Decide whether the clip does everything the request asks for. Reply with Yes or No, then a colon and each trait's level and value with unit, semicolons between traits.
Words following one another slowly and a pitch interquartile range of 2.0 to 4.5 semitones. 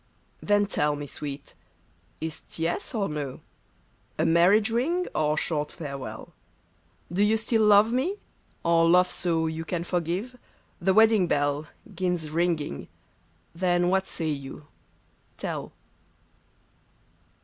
No: slow, 130 wpm; average, 5.0 semitones